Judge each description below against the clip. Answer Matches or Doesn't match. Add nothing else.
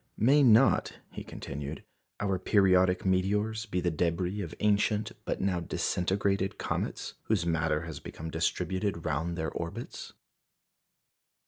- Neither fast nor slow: Doesn't match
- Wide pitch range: Doesn't match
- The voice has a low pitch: Matches